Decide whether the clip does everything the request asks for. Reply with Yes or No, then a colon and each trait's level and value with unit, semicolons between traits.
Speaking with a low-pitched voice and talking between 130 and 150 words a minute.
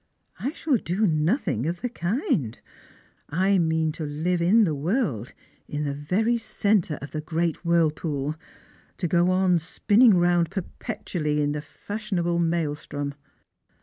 No: medium, 170 Hz; average, 145 wpm